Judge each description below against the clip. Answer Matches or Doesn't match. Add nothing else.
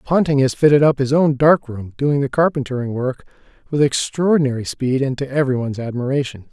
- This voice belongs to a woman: Doesn't match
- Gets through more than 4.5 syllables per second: Matches